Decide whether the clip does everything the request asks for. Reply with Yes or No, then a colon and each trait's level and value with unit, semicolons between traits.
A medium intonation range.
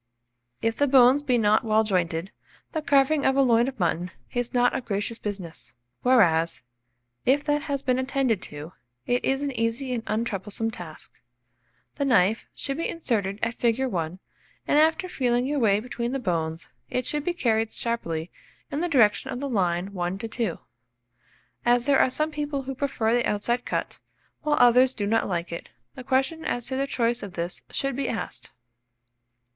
Yes: average, 5.0 semitones